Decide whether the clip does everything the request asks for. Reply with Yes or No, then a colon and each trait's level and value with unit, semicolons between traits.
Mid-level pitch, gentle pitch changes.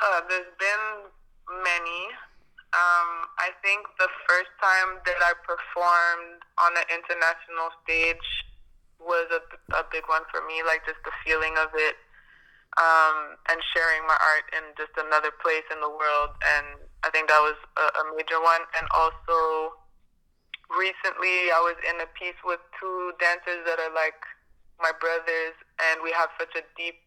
Yes: medium, 165 Hz; narrow, 1.9 semitones